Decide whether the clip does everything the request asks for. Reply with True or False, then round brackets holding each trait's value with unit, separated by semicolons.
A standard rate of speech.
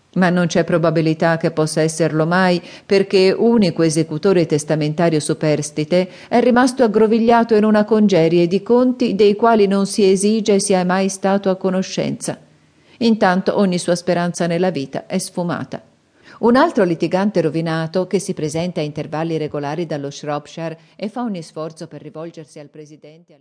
True (155 wpm)